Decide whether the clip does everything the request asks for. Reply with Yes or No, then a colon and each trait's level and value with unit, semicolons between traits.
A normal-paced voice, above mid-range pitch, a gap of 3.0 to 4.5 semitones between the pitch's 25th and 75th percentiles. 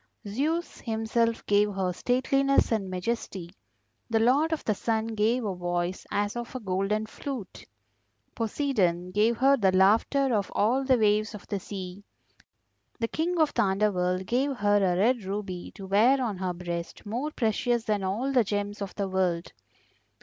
Yes: average, 165 wpm; high, 210 Hz; average, 4.2 semitones